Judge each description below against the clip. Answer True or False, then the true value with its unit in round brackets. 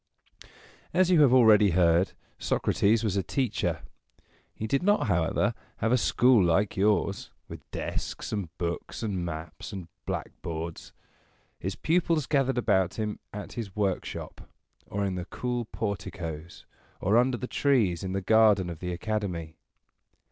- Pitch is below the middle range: True (100 Hz)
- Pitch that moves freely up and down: False (5.0 semitones)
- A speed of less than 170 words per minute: True (145 wpm)